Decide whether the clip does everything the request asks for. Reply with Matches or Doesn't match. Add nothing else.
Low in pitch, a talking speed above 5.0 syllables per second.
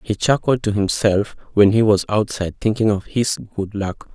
Doesn't match